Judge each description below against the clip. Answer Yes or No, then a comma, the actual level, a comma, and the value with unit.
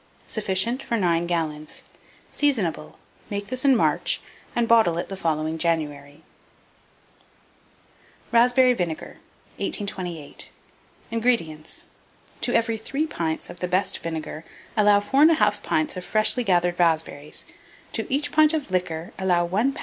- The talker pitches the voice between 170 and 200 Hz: Yes, high, 190 Hz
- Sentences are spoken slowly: Yes, slow, 130 wpm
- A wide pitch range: Yes, wide, 6.0 semitones